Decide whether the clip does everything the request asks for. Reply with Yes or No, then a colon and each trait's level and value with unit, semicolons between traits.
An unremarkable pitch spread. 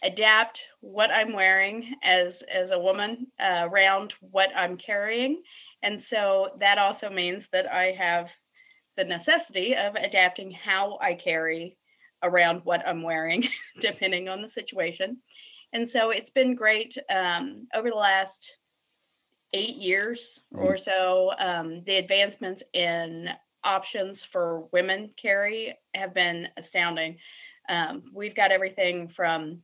Yes: average, 3.9 semitones